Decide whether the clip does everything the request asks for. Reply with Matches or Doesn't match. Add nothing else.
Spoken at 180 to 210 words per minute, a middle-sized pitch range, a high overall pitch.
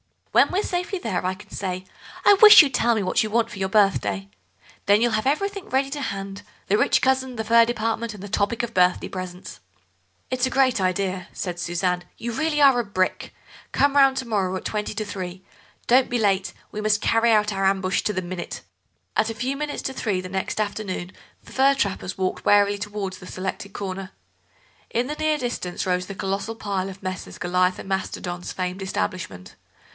Matches